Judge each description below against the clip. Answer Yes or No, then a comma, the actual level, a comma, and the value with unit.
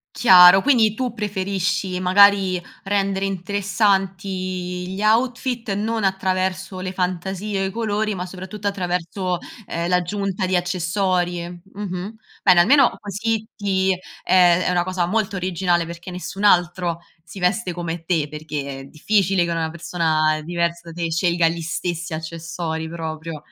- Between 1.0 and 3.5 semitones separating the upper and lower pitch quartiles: Yes, narrow, 2.4 semitones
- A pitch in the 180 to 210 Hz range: Yes, medium, 185 Hz